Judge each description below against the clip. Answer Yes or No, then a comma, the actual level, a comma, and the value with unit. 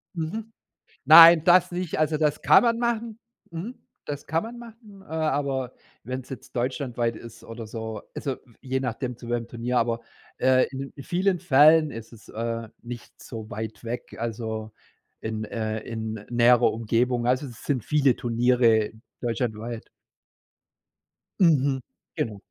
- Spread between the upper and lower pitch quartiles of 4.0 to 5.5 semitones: Yes, average, 5.1 semitones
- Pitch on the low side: Yes, low, 125 Hz